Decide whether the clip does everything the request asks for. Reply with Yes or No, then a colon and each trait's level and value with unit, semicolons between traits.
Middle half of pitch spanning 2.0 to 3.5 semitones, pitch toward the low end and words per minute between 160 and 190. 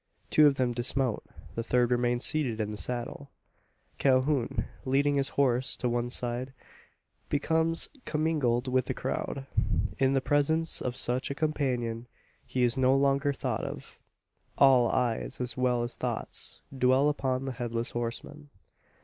No: narrow, 2.5 semitones; low, 130 Hz; average, 150 wpm